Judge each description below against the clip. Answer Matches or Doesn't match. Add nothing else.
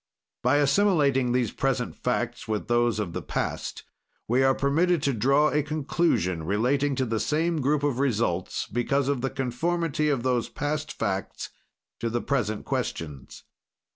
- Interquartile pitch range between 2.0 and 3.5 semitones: Doesn't match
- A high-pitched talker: Doesn't match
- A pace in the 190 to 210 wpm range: Doesn't match